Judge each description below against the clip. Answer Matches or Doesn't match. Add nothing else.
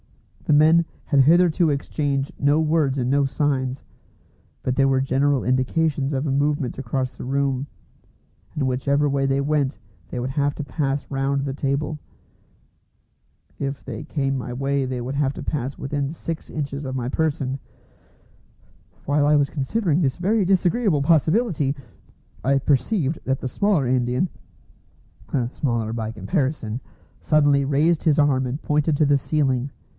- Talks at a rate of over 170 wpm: Doesn't match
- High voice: Doesn't match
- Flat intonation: Matches